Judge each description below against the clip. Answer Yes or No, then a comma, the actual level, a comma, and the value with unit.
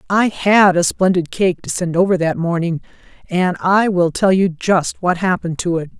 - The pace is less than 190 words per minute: No, average, 200 wpm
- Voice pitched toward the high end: No, medium, 180 Hz